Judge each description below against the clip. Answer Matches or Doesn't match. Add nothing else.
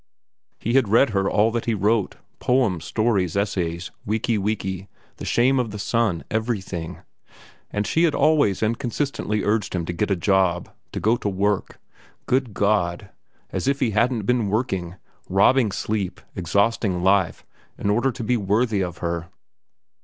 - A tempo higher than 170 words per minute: Doesn't match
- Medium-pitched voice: Doesn't match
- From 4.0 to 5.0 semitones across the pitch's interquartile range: Doesn't match